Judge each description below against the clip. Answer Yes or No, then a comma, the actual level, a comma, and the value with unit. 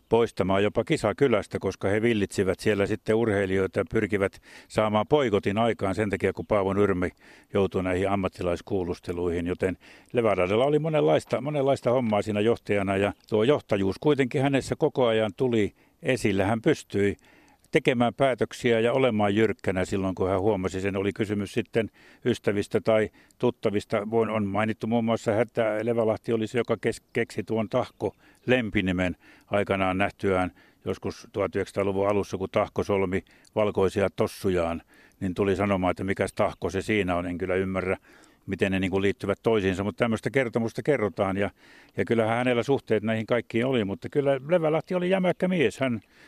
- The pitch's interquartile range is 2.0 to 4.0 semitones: Yes, average, 3.2 semitones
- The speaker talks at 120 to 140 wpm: No, average, 150 wpm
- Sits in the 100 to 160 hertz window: Yes, low, 105 Hz